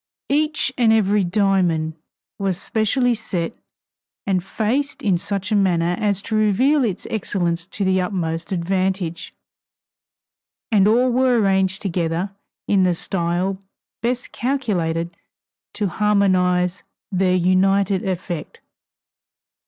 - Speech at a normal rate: No, slow, 110 wpm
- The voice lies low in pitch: No, high, 195 Hz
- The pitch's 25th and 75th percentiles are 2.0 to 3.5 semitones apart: Yes, average, 3.2 semitones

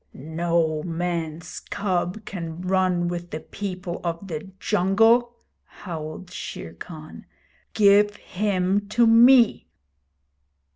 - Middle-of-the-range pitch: Yes, medium, 180 Hz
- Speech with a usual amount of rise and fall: Yes, average, 3.5 semitones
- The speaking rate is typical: No, slow, 100 wpm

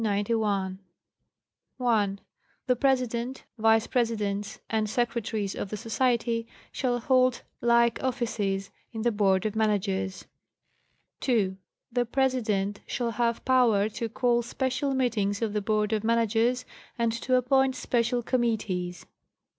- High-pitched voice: Yes, high, 230 Hz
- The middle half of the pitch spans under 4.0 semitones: Yes, average, 2.8 semitones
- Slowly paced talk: Yes, slow, 115 wpm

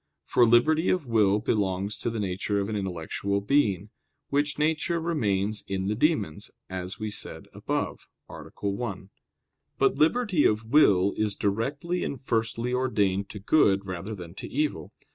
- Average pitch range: No, wide, 6.1 semitones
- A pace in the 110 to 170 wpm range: Yes, average, 155 wpm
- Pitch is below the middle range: Yes, low, 105 Hz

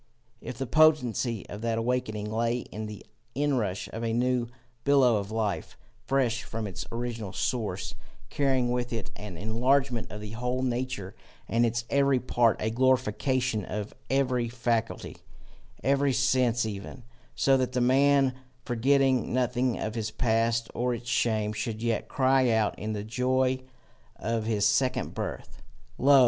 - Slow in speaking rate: No, average, 150 wpm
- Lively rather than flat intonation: No, average, 2.8 semitones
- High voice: No, low, 120 Hz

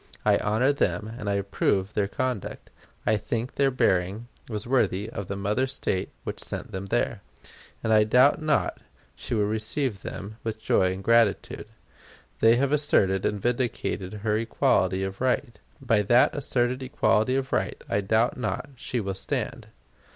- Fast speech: No, average, 165 wpm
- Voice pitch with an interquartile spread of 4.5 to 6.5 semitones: No, average, 4.0 semitones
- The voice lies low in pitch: Yes, low, 110 Hz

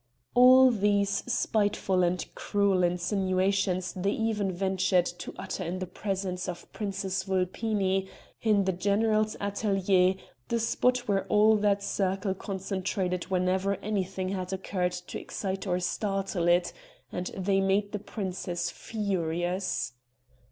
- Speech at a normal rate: No, slow, 125 wpm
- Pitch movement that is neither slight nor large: No, narrow, 1.8 semitones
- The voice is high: Yes, high, 195 Hz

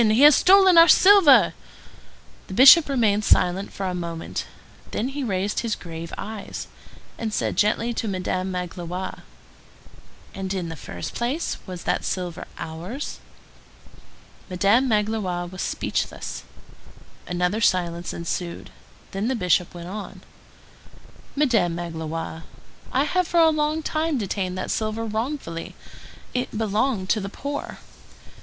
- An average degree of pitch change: No, wide, 6.2 semitones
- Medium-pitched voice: No, high, 205 Hz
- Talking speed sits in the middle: No, slow, 130 wpm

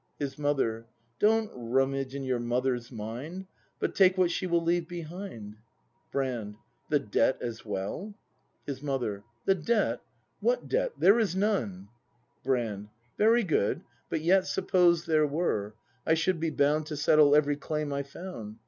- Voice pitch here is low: No, medium, 145 Hz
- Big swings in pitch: Yes, wide, 6.6 semitones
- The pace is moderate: Yes, average, 155 wpm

